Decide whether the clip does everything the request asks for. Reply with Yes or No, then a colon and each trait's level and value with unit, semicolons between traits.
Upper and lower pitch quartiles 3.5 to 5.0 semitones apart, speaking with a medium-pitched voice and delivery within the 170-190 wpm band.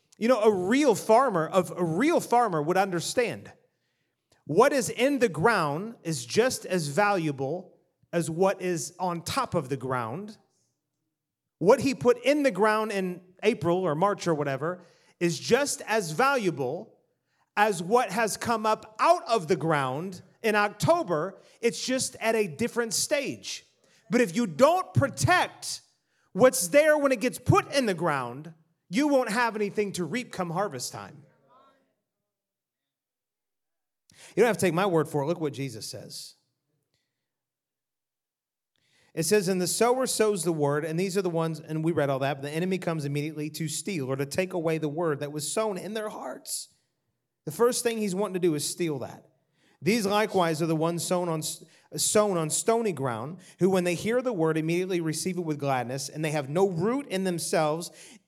No: wide, 5.5 semitones; medium, 180 Hz; average, 180 wpm